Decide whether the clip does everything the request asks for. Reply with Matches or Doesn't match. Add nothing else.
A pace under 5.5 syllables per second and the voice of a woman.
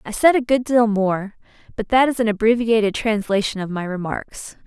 Matches